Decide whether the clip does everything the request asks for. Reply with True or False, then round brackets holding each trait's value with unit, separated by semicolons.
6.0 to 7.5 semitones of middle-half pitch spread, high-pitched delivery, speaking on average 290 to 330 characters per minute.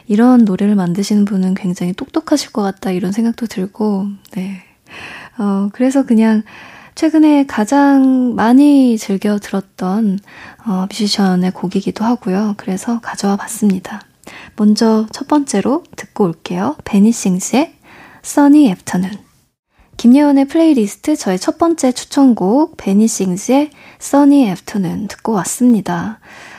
False (5.4 semitones; 215 Hz; 320 characters per minute)